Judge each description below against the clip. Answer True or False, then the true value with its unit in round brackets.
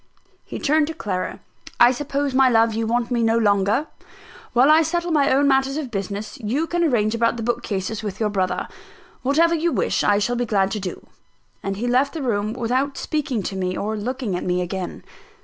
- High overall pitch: True (235 Hz)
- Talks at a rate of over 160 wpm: True (205 wpm)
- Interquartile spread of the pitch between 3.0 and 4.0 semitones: False (5.1 semitones)